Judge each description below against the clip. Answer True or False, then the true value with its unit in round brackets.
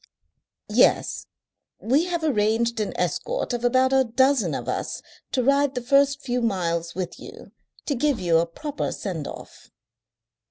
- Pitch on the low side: False (245 Hz)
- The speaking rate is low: False (155 wpm)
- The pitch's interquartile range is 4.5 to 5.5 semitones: True (5.1 semitones)